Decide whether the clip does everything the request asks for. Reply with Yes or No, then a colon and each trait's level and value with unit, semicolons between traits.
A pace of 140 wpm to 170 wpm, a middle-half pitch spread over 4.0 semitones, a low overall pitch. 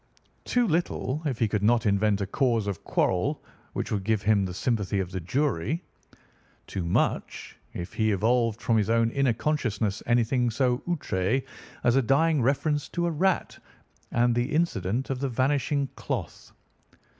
Yes: average, 165 wpm; average, 4.9 semitones; low, 120 Hz